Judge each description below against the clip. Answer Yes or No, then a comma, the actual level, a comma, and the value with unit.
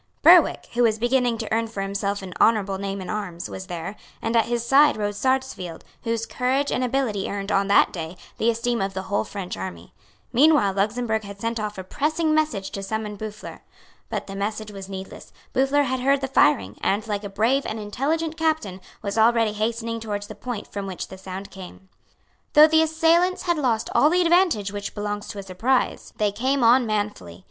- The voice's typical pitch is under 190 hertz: No, high, 215 Hz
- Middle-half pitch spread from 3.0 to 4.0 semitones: No, average, 4.5 semitones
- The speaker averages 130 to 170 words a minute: No, average, 200 wpm